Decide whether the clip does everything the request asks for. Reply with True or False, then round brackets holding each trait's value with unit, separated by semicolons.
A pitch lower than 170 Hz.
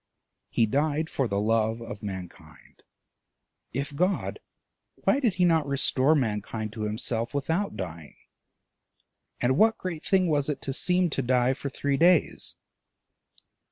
True (135 Hz)